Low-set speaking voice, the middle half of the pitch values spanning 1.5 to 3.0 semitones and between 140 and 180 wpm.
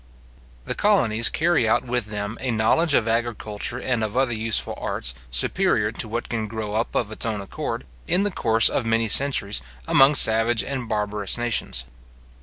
Yes: low, 115 Hz; narrow, 2.5 semitones; average, 175 wpm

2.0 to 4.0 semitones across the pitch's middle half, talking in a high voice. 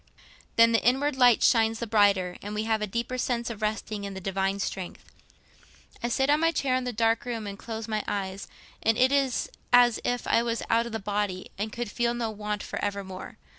Yes: average, 2.8 semitones; high, 225 Hz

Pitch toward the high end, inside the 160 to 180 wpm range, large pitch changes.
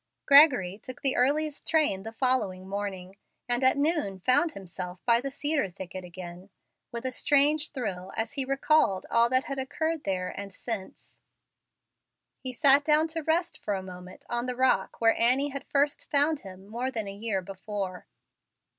Yes: high, 240 Hz; average, 170 wpm; wide, 6.6 semitones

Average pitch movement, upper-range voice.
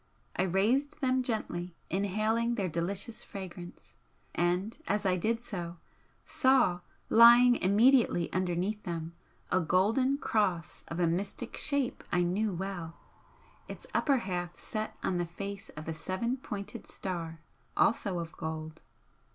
Yes: average, 4.7 semitones; high, 195 Hz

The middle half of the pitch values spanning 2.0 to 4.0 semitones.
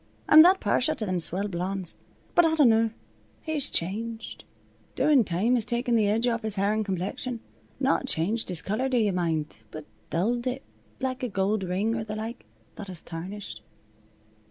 No: average, 4.5 semitones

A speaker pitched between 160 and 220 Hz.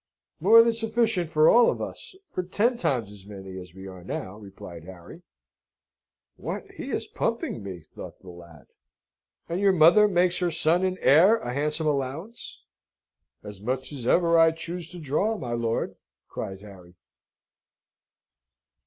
No: medium, 150 Hz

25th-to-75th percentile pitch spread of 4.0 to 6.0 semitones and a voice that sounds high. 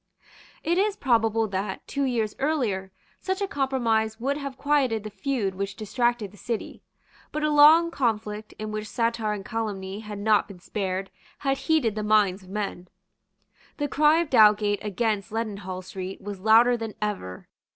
Yes: average, 4.5 semitones; high, 220 Hz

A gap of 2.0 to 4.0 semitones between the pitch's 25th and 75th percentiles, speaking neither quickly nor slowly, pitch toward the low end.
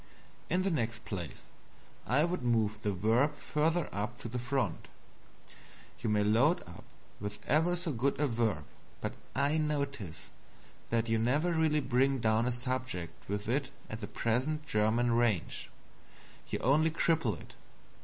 No: wide, 5.4 semitones; average, 155 wpm; low, 120 Hz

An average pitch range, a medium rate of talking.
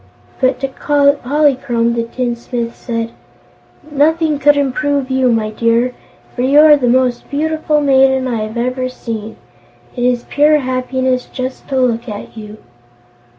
Yes: average, 3.0 semitones; average, 145 wpm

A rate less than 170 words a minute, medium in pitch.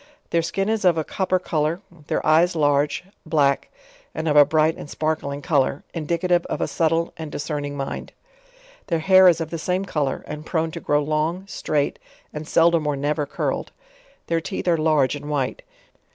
No: average, 185 wpm; medium, 155 Hz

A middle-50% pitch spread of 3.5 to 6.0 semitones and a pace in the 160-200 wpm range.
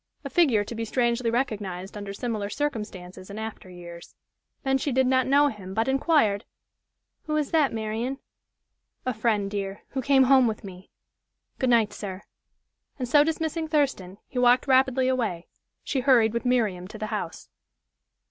Yes: average, 4.7 semitones; average, 165 wpm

